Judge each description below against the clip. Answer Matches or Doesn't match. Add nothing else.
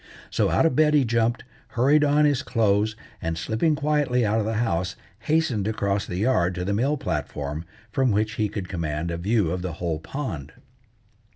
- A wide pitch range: Matches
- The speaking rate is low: Doesn't match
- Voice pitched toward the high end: Doesn't match